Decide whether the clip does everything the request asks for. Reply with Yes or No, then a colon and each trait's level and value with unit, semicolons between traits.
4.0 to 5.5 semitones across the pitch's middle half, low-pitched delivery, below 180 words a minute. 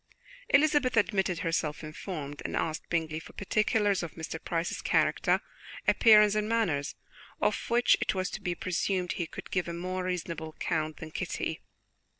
No: average, 4.3 semitones; medium, 180 Hz; average, 160 wpm